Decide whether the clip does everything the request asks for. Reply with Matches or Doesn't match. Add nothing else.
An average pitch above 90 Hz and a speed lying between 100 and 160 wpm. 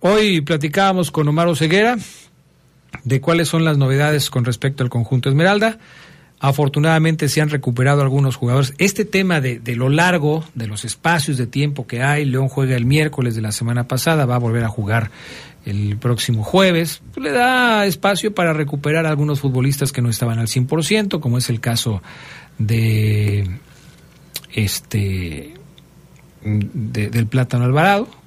Matches